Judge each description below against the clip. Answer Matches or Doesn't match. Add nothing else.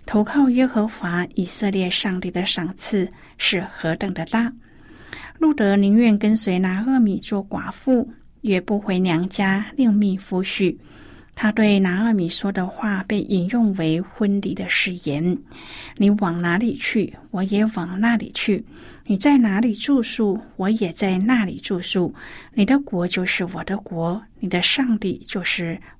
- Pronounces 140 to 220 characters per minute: Matches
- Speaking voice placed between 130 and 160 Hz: Doesn't match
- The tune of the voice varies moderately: Matches